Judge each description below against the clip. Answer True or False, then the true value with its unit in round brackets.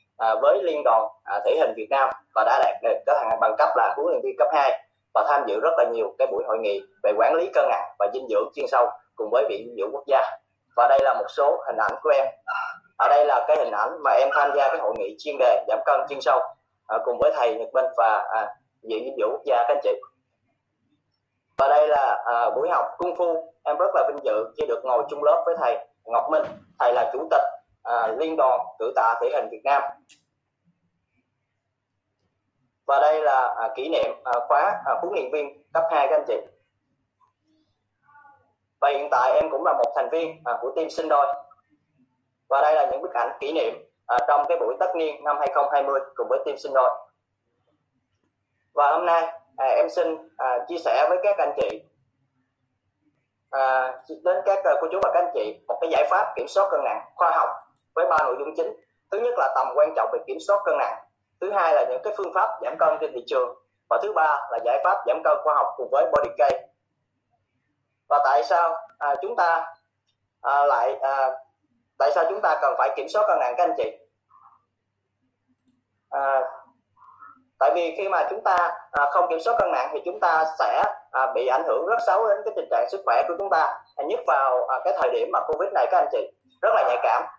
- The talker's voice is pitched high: False (160 Hz)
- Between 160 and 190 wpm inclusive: False (220 wpm)